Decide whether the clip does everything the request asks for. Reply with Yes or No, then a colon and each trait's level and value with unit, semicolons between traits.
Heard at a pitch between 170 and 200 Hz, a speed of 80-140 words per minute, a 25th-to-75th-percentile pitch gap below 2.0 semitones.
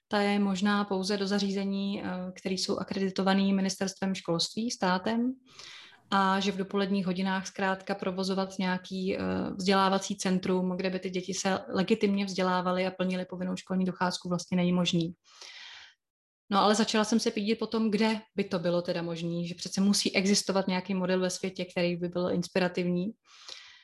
No: high, 190 Hz; average, 155 wpm; narrow, 1.6 semitones